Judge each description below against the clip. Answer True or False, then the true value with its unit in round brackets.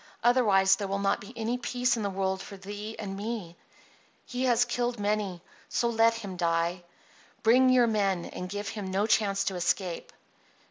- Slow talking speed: False (180 wpm)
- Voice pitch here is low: False (205 Hz)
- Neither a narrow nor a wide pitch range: True (3.2 semitones)